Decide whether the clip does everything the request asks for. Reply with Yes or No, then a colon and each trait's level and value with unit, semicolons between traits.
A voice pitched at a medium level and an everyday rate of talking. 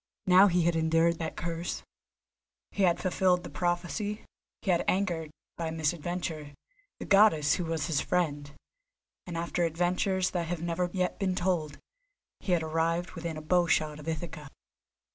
Yes: medium, 170 Hz; average, 155 wpm